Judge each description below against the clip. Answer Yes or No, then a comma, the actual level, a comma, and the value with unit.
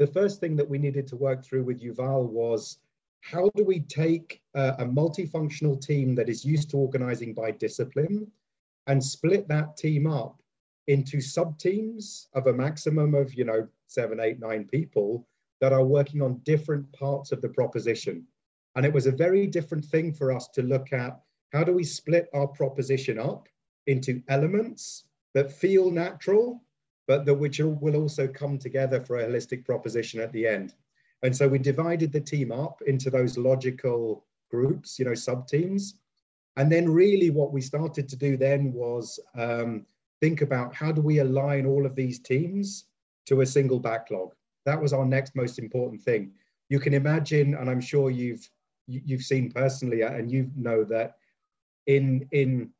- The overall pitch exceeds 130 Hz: Yes, medium, 140 Hz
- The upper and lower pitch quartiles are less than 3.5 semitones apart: Yes, average, 3.0 semitones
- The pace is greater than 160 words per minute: Yes, average, 175 wpm